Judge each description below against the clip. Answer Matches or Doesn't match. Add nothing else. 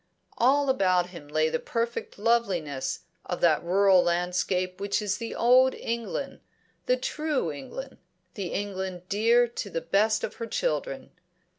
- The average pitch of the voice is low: Doesn't match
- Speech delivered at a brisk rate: Doesn't match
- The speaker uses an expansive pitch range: Doesn't match